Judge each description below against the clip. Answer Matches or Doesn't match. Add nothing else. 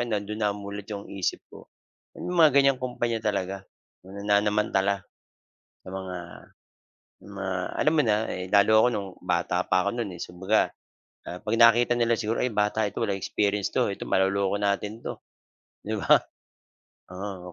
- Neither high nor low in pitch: Doesn't match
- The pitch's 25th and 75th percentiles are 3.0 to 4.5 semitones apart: Doesn't match